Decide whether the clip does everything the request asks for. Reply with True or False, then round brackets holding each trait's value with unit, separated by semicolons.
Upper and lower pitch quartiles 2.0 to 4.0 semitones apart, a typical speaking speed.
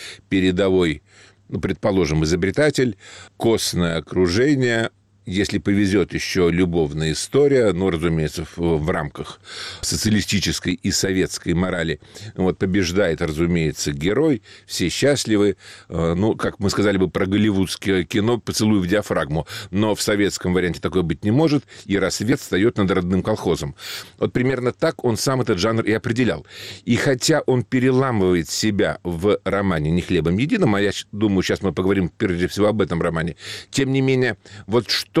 True (3.5 semitones; 145 wpm)